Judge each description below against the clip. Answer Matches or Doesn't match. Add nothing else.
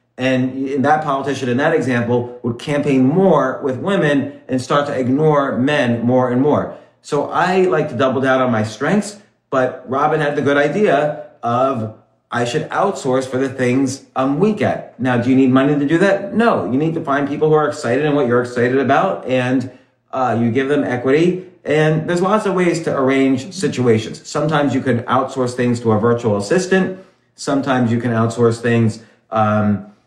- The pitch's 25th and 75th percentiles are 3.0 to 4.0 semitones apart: Matches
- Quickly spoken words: Doesn't match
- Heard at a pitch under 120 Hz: Doesn't match